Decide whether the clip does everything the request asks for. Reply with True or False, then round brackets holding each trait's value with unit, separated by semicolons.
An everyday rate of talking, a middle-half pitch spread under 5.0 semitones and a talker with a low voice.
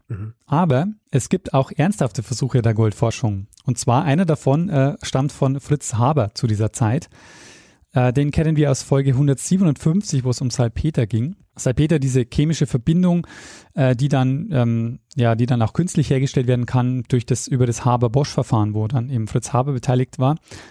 True (175 wpm; 2.9 semitones; 130 Hz)